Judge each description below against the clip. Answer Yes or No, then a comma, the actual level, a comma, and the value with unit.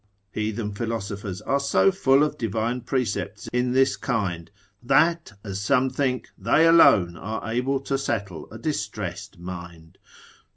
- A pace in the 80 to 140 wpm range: Yes, slow, 135 wpm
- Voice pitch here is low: Yes, low, 115 Hz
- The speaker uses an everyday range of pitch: Yes, average, 5.0 semitones